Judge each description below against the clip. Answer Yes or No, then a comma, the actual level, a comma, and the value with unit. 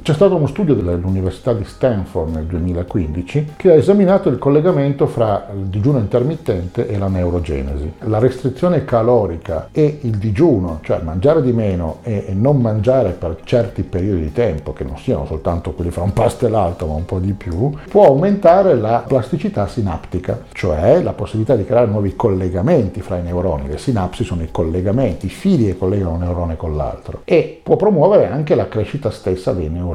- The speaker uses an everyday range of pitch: No, wide, 6.5 semitones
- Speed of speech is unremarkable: No, fast, 180 wpm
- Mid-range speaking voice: No, low, 105 Hz